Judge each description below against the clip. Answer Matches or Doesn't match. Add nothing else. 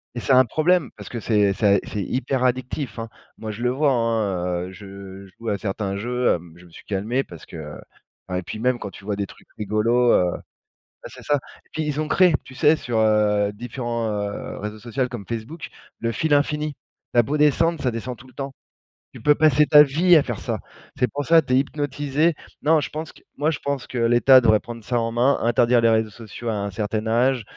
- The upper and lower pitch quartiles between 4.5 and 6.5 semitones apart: Matches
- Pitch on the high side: Doesn't match